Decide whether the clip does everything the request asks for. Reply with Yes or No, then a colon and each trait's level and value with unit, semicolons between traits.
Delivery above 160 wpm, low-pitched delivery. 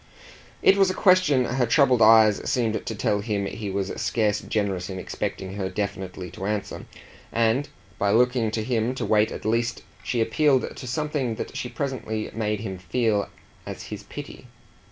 Yes: average, 175 wpm; low, 110 Hz